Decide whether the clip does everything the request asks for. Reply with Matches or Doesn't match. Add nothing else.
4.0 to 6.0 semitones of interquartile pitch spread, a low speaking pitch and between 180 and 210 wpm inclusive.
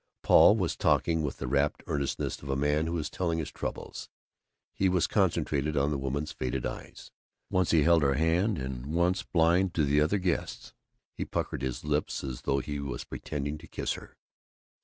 Doesn't match